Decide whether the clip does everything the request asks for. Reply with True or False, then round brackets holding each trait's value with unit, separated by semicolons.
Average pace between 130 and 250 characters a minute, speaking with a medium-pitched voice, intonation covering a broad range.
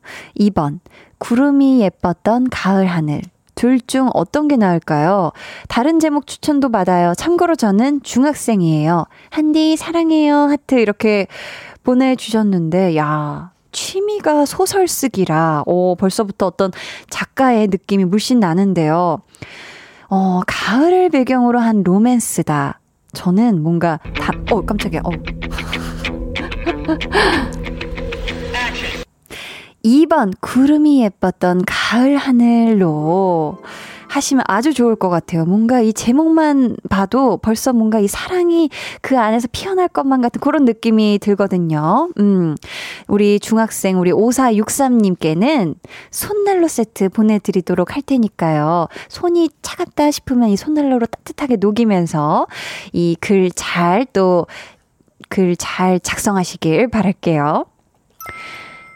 False (235 characters per minute; 215 Hz; 6.8 semitones)